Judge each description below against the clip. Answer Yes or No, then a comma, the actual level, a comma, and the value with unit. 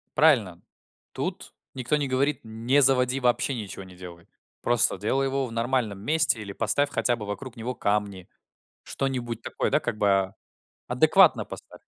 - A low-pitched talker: Yes, low, 120 Hz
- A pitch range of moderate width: Yes, average, 4.5 semitones